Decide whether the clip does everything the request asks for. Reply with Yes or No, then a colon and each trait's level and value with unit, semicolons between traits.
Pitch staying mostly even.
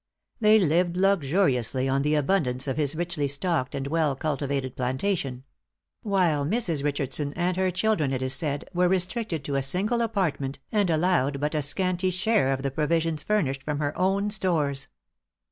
No: average, 5.2 semitones